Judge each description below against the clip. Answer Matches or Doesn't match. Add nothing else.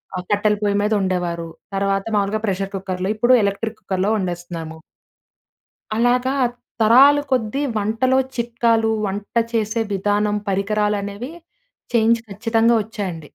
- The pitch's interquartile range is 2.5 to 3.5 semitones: Matches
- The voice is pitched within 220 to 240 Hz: Doesn't match